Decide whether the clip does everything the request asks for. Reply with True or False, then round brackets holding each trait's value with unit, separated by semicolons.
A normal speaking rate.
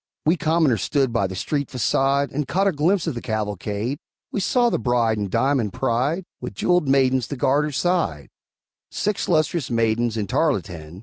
True (180 wpm)